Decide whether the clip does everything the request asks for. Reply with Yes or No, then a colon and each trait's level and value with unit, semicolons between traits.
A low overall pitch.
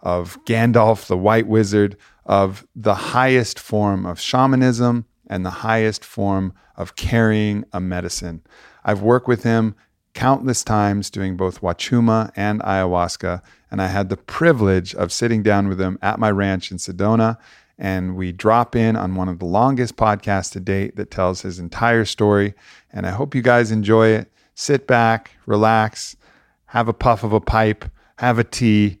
Yes: low, 105 Hz